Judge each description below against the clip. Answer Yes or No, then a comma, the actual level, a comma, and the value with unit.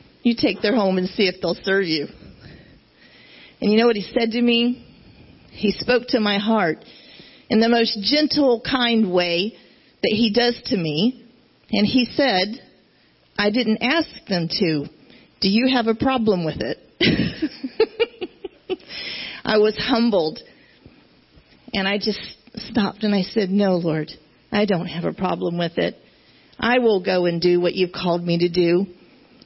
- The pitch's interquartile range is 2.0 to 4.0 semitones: No, average, 4.8 semitones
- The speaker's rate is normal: Yes, average, 160 wpm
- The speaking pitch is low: No, high, 215 Hz